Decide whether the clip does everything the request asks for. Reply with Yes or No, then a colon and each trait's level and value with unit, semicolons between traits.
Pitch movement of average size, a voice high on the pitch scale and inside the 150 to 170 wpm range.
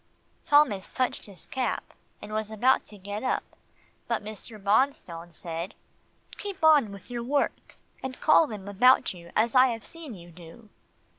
Yes: average, 4.9 semitones; high, 220 Hz; average, 160 wpm